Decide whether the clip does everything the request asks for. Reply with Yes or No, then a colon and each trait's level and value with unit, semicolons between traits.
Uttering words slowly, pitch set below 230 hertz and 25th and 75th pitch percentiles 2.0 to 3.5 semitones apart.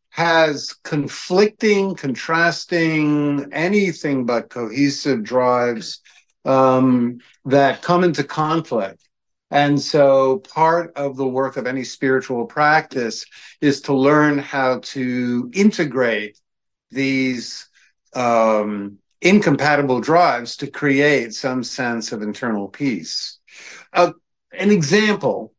No: slow, 100 wpm; medium, 140 Hz; average, 4.1 semitones